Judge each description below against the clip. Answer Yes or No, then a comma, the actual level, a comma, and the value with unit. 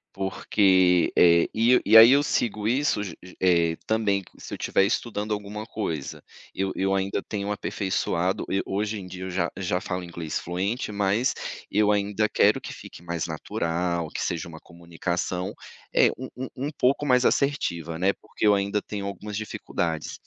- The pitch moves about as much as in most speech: Yes, average, 3.3 semitones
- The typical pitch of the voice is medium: No, low, 100 Hz